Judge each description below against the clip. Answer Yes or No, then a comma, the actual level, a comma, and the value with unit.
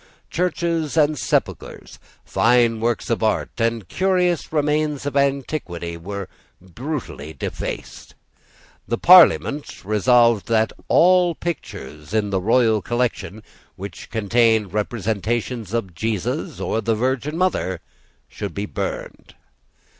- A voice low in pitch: Yes, low, 115 Hz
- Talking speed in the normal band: No, slow, 115 wpm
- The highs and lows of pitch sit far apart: Yes, wide, 6.1 semitones